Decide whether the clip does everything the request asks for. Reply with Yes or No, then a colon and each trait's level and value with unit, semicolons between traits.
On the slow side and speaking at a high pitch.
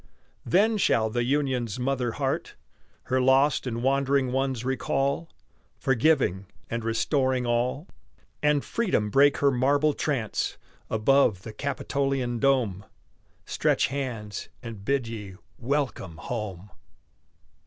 No: slow, 110 wpm; low, 130 Hz